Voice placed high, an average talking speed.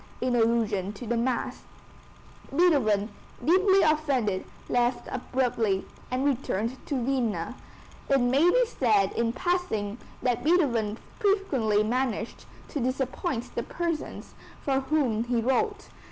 No: very high, 250 Hz; slow, 120 wpm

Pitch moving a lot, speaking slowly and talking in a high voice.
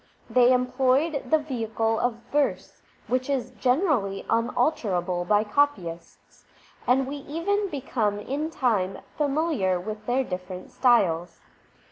Yes: wide, 5.7 semitones; slow, 115 wpm; high, 245 Hz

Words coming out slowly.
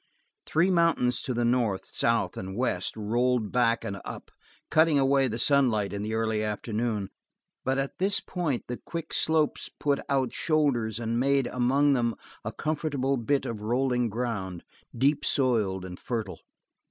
No: average, 155 wpm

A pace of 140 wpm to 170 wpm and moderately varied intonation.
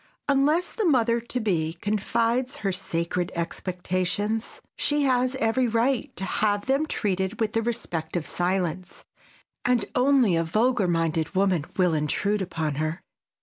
No: average, 145 wpm; wide, 5.7 semitones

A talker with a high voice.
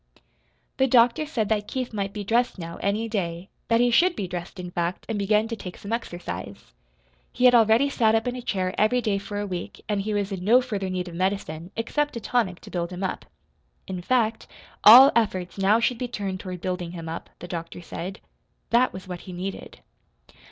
Yes: high, 200 Hz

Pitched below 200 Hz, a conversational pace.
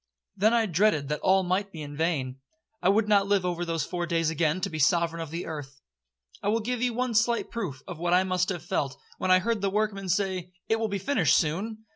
No: medium, 185 Hz; fast, 240 wpm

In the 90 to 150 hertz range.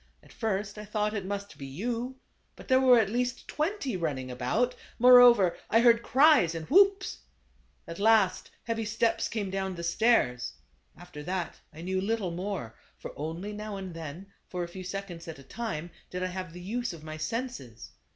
No: high, 195 Hz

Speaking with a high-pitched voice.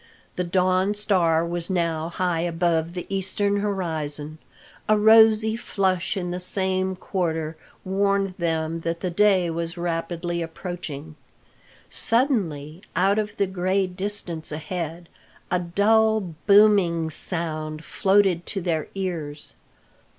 No: medium, 180 Hz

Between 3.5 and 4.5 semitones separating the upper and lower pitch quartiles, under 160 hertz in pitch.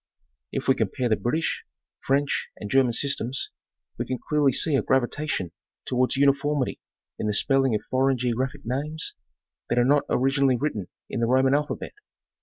No: narrow, 2.5 semitones; low, 135 Hz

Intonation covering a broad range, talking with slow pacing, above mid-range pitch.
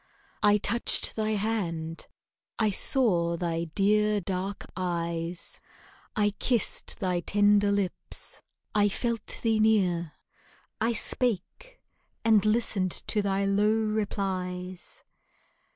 No: average, 3.1 semitones; slow, 105 wpm; high, 205 Hz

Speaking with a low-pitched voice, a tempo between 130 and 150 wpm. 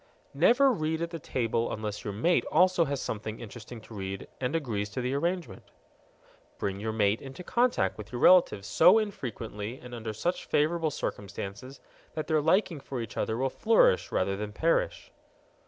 No: low, 125 Hz; average, 170 wpm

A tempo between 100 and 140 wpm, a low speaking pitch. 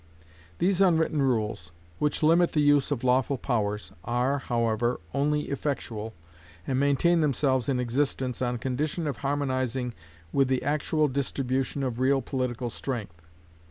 Yes: slow, 135 wpm; low, 130 Hz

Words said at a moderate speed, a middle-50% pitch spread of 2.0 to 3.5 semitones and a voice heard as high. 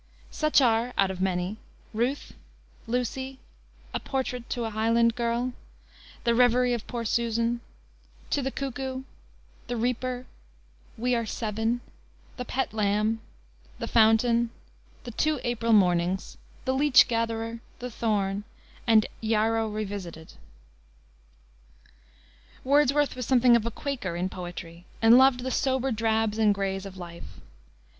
No: slow, 130 wpm; average, 2.8 semitones; high, 230 Hz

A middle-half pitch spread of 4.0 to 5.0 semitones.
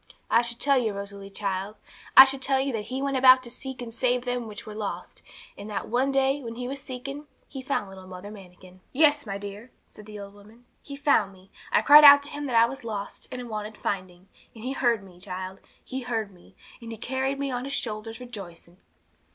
Yes: average, 4.7 semitones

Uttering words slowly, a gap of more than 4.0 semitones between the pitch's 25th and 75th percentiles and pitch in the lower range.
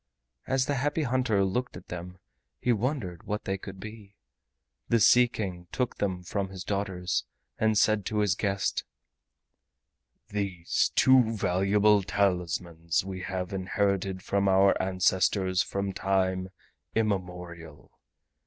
No: slow, 125 wpm; narrow, 2.5 semitones; very low, 95 Hz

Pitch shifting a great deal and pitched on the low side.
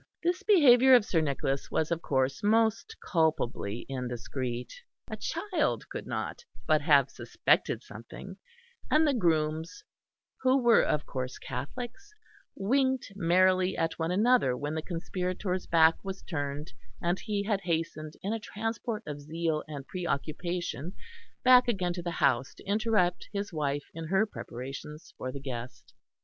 No: wide, 6.5 semitones; medium, 170 Hz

